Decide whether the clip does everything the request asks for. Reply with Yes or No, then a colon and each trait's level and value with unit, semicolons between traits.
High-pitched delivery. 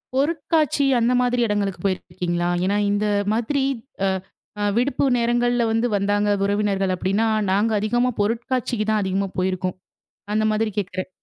Yes: high, 210 Hz